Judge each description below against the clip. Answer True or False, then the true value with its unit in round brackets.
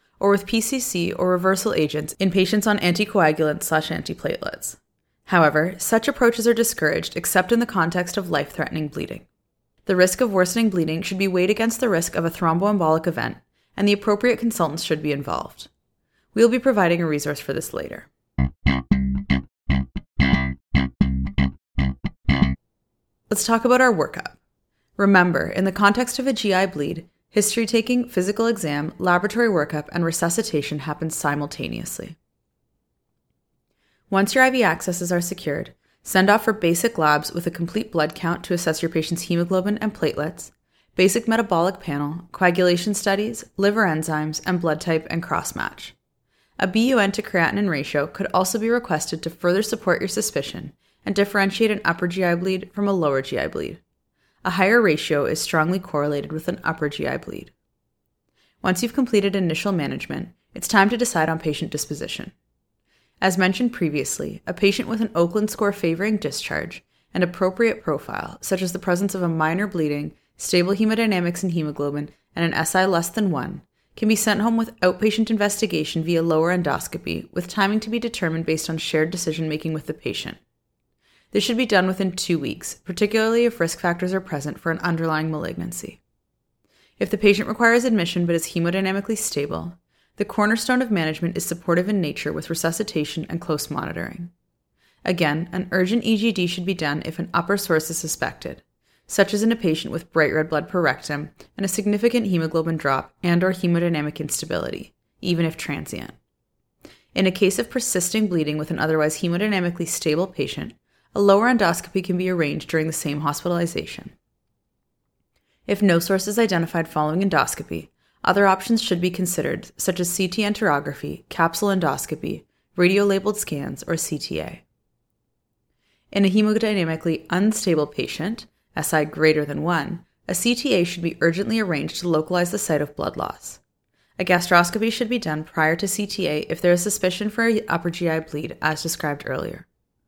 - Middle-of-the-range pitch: True (180 Hz)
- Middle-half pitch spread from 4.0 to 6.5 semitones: True (4.4 semitones)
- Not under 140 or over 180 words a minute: True (160 wpm)